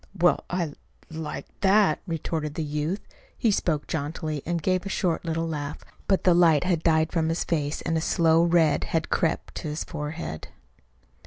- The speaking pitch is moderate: Yes, medium, 165 Hz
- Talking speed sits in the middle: Yes, average, 180 wpm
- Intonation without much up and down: Yes, narrow, 2.1 semitones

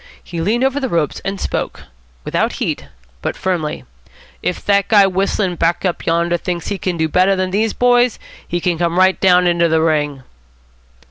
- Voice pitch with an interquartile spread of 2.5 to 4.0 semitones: Yes, average, 2.8 semitones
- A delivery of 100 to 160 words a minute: No, average, 185 wpm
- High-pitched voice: No, medium, 180 Hz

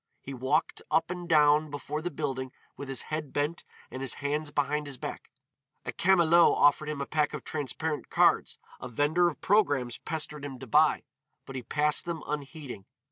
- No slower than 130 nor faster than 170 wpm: No, average, 185 wpm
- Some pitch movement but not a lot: No, narrow, 2.3 semitones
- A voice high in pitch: No, medium, 150 Hz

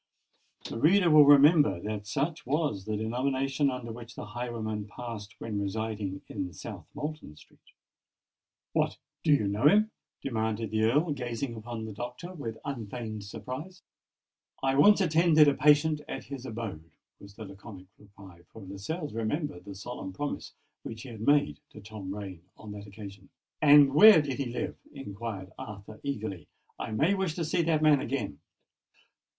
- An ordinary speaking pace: Yes, average, 160 wpm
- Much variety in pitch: Yes, wide, 5.9 semitones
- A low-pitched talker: Yes, low, 115 Hz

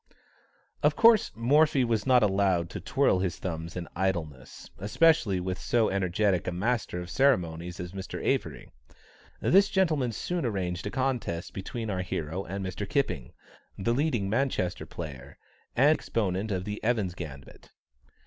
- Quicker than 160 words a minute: No, average, 150 wpm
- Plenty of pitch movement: Yes, wide, 5.7 semitones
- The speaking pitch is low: Yes, low, 100 Hz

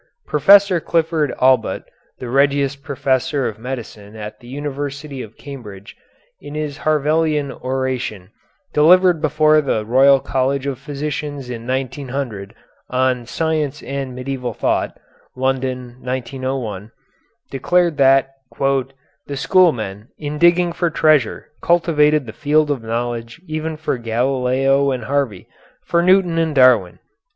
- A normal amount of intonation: Yes, average, 3.2 semitones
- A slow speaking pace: Yes, slow, 120 wpm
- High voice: No, low, 135 Hz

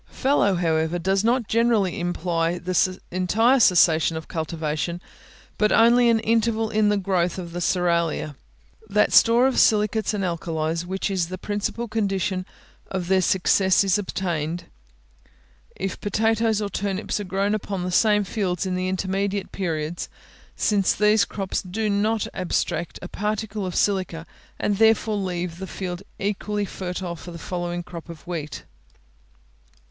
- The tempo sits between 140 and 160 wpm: Yes, average, 150 wpm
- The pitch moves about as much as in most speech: Yes, average, 3.2 semitones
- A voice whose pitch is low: No, high, 190 Hz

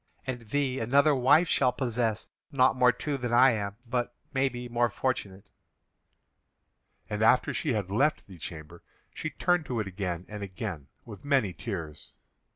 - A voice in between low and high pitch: No, low, 120 Hz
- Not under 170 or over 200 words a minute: No, average, 160 wpm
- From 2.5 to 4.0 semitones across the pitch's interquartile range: No, average, 4.7 semitones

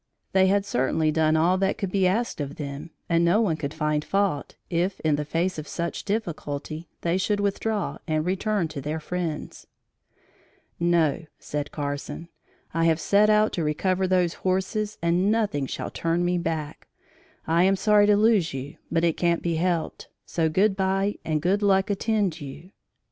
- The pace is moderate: Yes, average, 175 wpm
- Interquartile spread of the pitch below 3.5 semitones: No, average, 3.8 semitones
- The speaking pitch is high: No, medium, 170 Hz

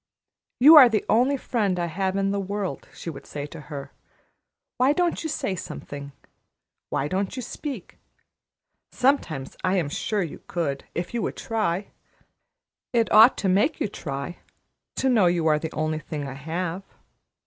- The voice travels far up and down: Yes, wide, 6.3 semitones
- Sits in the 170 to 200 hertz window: Yes, medium, 185 Hz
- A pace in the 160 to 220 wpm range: Yes, average, 170 wpm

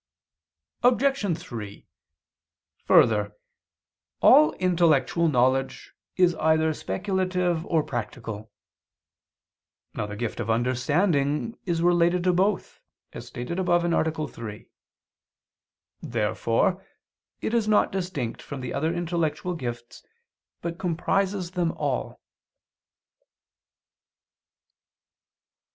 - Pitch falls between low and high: Yes, medium, 165 Hz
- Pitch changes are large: Yes, wide, 6.4 semitones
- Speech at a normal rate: No, slow, 90 wpm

